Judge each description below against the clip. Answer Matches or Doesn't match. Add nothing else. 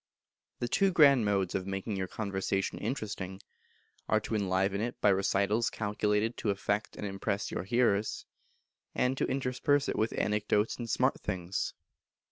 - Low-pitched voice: Matches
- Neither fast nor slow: Matches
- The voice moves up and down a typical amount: Matches